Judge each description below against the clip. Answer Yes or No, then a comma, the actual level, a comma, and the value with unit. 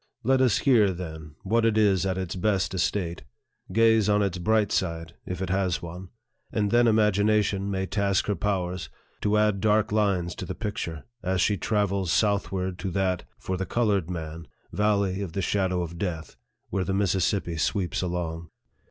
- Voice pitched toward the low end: Yes, very low, 95 Hz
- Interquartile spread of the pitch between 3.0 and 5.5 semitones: No, narrow, 2.6 semitones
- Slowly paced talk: No, average, 175 wpm